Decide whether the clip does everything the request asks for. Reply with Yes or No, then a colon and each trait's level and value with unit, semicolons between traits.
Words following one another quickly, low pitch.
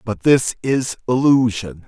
No: slow, 130 wpm; low, 125 Hz